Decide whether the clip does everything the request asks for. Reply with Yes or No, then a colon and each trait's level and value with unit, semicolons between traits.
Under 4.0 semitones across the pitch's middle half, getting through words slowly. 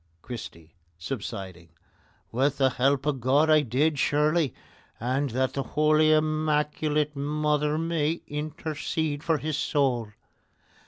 Yes: average, 2.8 semitones; slow, 115 wpm